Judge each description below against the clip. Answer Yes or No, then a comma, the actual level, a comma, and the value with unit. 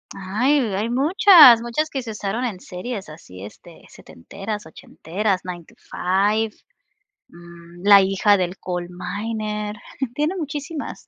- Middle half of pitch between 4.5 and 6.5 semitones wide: Yes, average, 5.0 semitones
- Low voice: No, high, 210 Hz